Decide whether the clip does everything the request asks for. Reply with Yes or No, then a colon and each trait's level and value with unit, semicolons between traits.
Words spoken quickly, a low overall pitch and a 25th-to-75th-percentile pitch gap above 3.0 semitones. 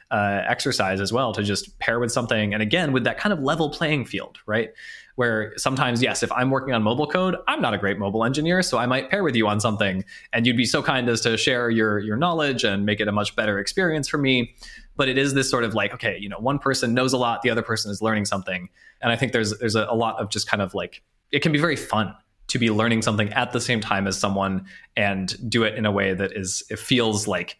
Yes: fast, 265 wpm; low, 115 Hz; average, 4.1 semitones